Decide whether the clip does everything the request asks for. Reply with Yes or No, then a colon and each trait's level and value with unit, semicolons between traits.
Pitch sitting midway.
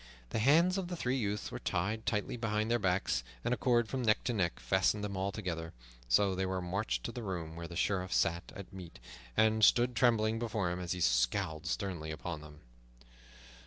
No: low, 100 Hz